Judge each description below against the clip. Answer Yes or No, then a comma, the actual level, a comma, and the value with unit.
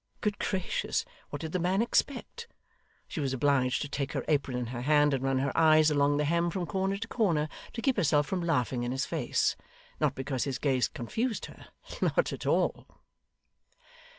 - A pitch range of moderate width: No, wide, 5.8 semitones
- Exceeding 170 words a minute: Yes, average, 190 wpm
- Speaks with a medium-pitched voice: Yes, medium, 150 Hz